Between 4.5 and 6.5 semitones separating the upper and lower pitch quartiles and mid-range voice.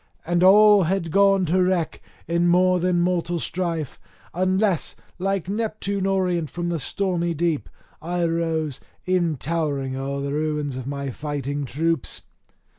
No: average, 3.4 semitones; medium, 170 Hz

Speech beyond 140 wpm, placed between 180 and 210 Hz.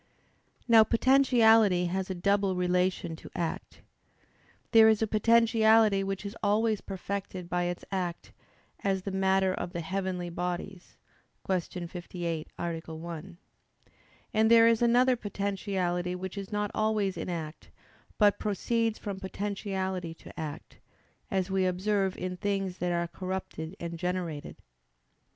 No: slow, 135 wpm; high, 190 Hz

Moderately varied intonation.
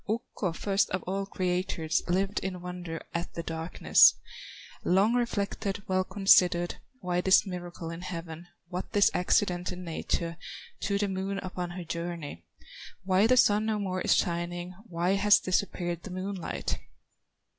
No: narrow, 2.1 semitones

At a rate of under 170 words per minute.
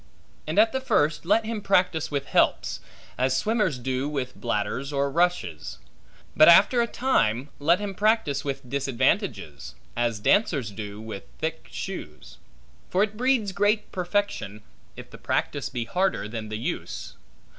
Yes: average, 150 wpm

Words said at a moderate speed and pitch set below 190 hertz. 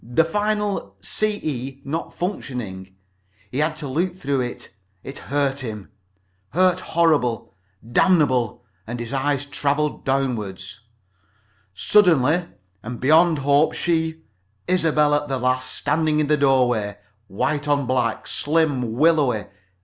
No: slow, 120 wpm; medium, 140 Hz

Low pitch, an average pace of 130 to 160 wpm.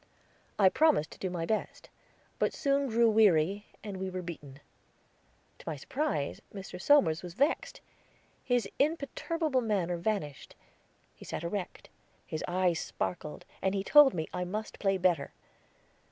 No: high, 190 Hz; average, 145 wpm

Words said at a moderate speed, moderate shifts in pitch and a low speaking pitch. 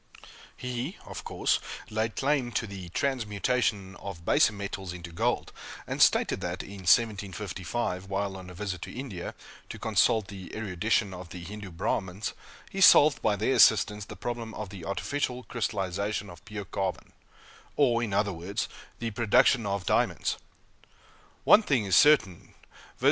Yes: average, 155 wpm; average, 3.7 semitones; low, 100 Hz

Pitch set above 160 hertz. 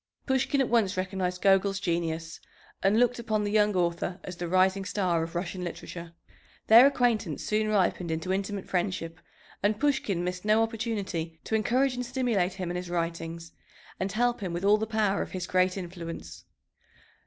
Yes: high, 190 Hz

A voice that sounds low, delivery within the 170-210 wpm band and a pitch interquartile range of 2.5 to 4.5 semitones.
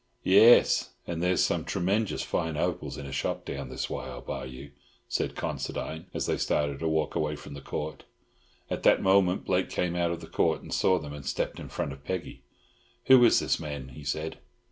Yes: very low, 80 Hz; average, 200 wpm; average, 4.2 semitones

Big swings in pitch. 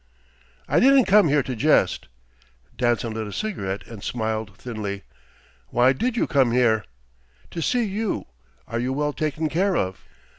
Yes: wide, 7.3 semitones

